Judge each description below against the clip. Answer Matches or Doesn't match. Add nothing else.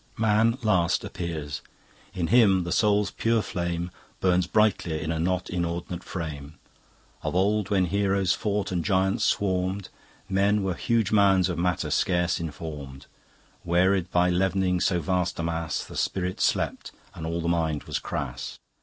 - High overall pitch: Doesn't match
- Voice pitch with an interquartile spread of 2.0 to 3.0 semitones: Matches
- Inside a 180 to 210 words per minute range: Doesn't match